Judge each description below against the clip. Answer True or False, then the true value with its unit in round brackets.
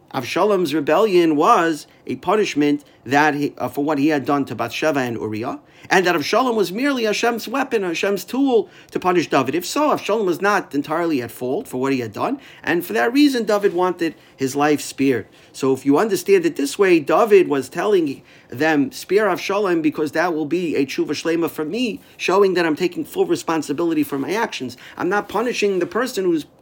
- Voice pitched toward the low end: False (175 Hz)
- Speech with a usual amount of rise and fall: False (8.9 semitones)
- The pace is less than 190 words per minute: False (200 wpm)